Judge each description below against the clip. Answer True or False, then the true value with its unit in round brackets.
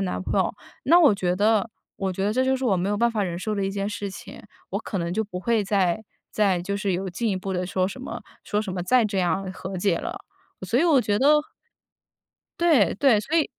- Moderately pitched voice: False (200 Hz)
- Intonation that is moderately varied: True (3.7 semitones)